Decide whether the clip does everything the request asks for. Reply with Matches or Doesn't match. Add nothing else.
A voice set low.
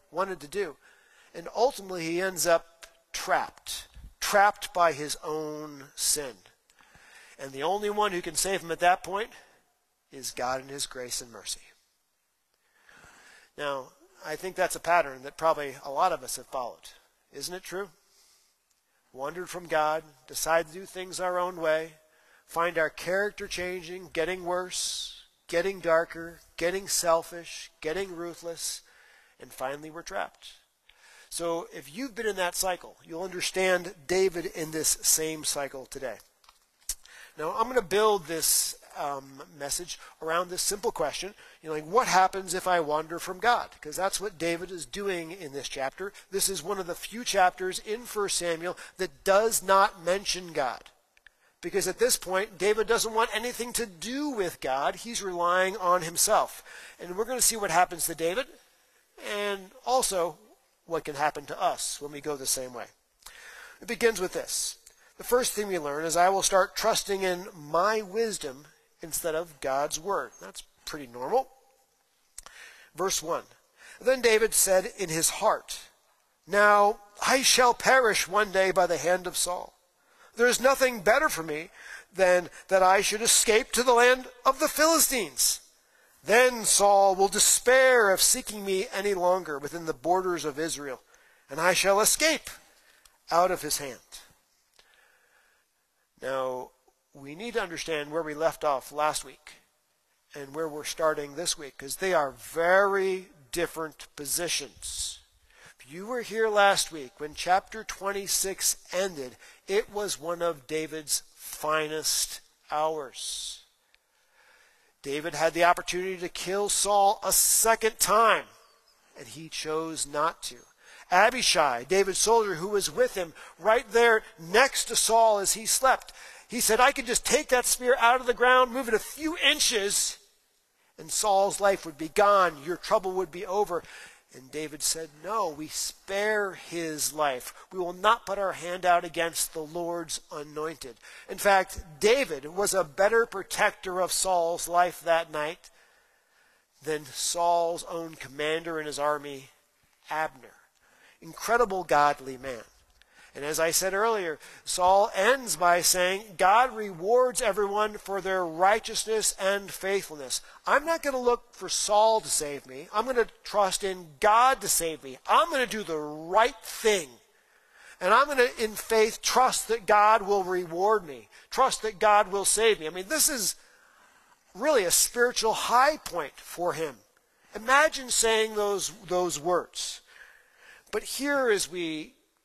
Doesn't match